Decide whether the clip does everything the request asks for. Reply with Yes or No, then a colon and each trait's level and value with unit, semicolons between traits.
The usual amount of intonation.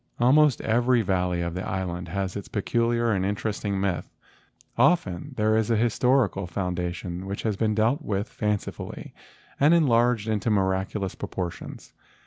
Yes: average, 3.9 semitones